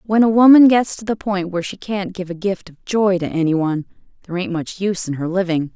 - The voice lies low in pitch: No, medium, 185 Hz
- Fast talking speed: Yes, fast, 250 wpm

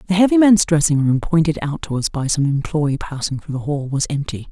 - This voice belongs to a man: No, female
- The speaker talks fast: Yes, fast, 240 wpm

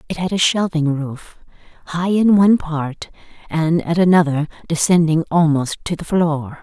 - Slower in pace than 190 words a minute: Yes, average, 155 wpm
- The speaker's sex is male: No, female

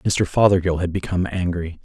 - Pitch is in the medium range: No, very low, 90 Hz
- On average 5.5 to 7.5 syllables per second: Yes, 5.6 syllables/s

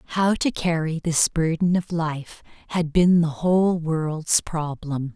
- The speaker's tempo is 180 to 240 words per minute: No, average, 150 wpm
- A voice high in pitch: No, medium, 165 Hz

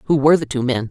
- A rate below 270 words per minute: No, fast, 330 wpm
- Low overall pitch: No, medium, 145 Hz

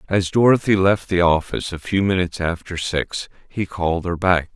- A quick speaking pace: No, average, 185 wpm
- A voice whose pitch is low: Yes, very low, 90 Hz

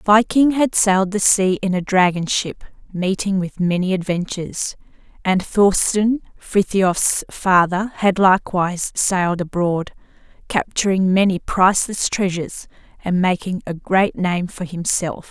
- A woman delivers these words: Yes, female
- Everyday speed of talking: No, slow, 125 wpm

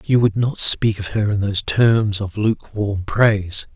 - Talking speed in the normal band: Yes, average, 190 wpm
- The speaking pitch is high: No, low, 105 Hz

